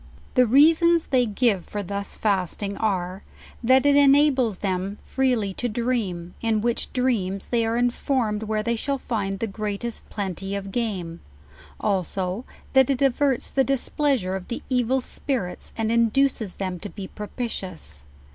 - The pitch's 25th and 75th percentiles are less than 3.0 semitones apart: No, average, 4.6 semitones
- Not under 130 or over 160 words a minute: Yes, average, 150 wpm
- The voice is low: No, high, 220 Hz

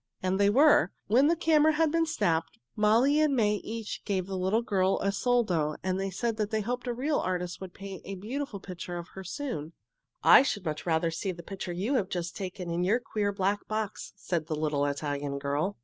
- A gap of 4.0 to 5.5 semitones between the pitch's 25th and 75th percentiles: Yes, average, 5.0 semitones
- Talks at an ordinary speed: No, fast, 210 wpm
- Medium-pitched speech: No, high, 195 Hz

